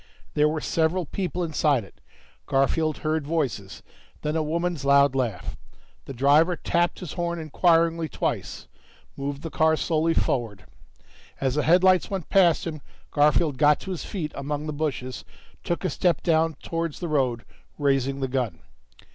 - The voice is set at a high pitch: No, medium, 155 Hz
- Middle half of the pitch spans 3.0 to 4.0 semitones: Yes, average, 3.3 semitones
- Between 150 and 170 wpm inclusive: Yes, average, 155 wpm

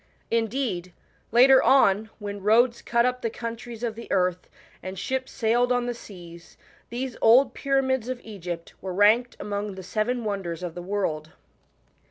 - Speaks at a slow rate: No, average, 160 wpm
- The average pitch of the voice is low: No, high, 220 Hz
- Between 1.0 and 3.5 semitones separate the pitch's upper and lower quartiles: No, average, 4.3 semitones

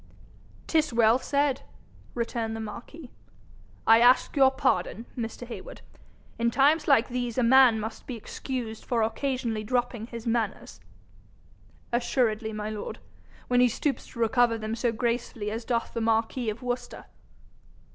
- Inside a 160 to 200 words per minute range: No, average, 145 wpm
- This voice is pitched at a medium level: No, high, 235 Hz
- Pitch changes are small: Yes, narrow, 2.2 semitones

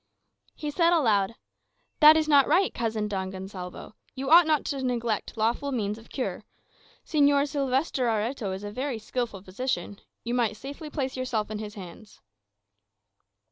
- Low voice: No, high, 240 Hz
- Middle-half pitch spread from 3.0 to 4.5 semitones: No, average, 5.2 semitones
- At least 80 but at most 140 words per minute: No, average, 155 wpm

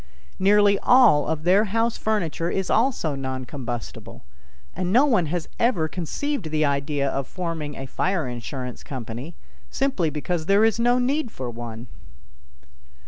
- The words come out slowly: No, average, 145 wpm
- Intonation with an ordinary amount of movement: No, wide, 7.6 semitones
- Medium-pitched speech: Yes, medium, 165 Hz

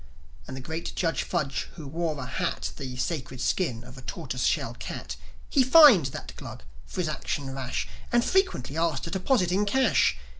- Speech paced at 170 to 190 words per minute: Yes, average, 185 wpm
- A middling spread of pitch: No, wide, 6.2 semitones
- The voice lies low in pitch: No, medium, 160 Hz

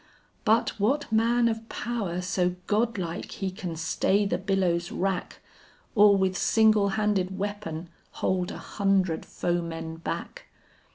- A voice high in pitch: Yes, high, 195 Hz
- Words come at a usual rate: No, slow, 125 wpm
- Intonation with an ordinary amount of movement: Yes, average, 3.1 semitones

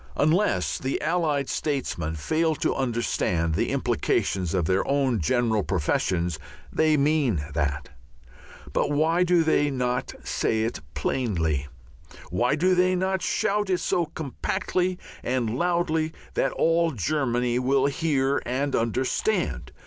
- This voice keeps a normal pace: No, slow, 125 wpm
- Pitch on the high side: No, low, 135 Hz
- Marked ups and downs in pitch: Yes, wide, 6.5 semitones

